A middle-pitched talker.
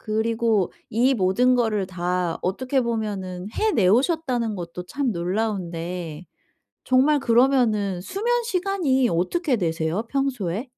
No: high, 220 Hz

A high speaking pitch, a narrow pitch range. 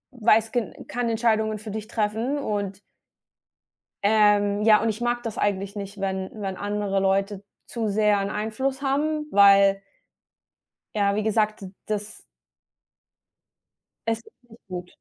Yes: high, 210 Hz; narrow, 2.1 semitones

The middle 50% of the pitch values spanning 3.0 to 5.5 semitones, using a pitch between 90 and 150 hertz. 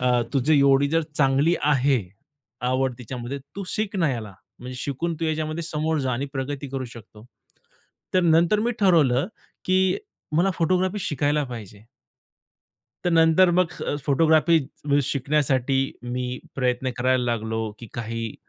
Yes: average, 4.5 semitones; medium, 140 Hz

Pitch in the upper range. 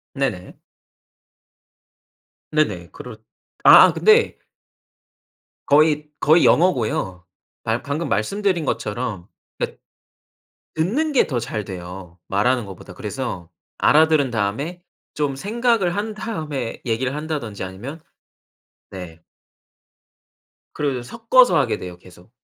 No: low, 135 Hz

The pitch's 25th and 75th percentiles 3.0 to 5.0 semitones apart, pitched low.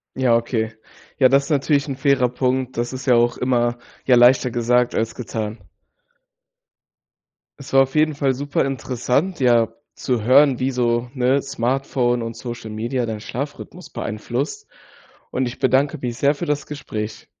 No: narrow, 2.6 semitones; low, 125 Hz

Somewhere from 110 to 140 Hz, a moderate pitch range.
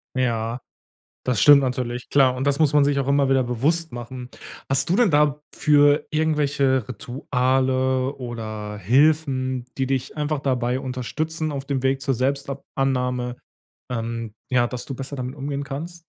No: low, 135 Hz; narrow, 2.3 semitones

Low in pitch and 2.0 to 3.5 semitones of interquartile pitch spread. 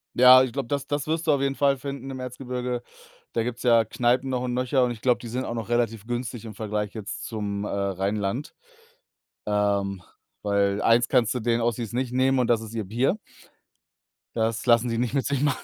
Yes: low, 120 Hz; average, 2.8 semitones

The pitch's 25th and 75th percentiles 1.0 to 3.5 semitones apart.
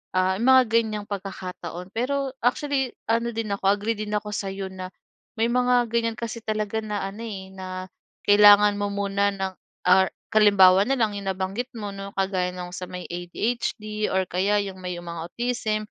Yes: average, 3.1 semitones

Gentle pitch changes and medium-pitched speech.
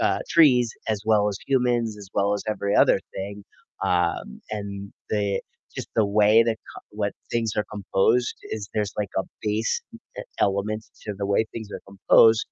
No: narrow, 1.8 semitones; low, 105 Hz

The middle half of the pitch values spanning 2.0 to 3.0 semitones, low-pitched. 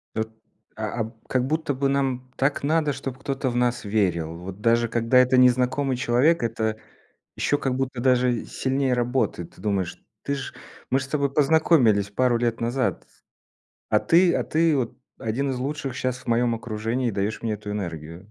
No: average, 3.5 semitones; low, 125 Hz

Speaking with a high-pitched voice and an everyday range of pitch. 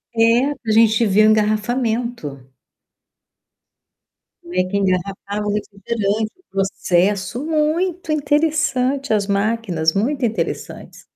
Yes: high, 220 Hz; average, 4.6 semitones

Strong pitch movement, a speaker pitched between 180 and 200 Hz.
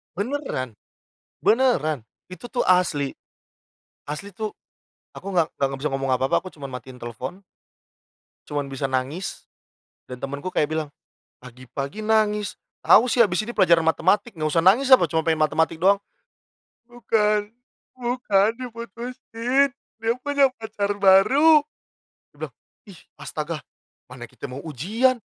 Yes: wide, 7.6 semitones; high, 190 Hz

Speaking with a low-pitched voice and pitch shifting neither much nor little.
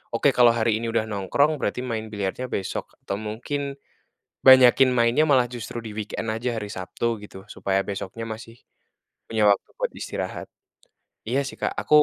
Yes: low, 115 Hz; average, 3.4 semitones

